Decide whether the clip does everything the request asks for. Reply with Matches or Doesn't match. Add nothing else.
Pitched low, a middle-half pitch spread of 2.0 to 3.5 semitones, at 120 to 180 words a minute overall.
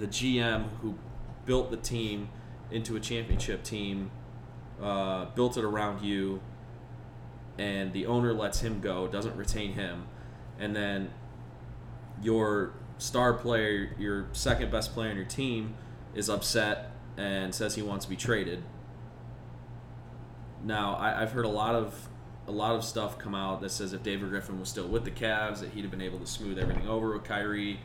Matches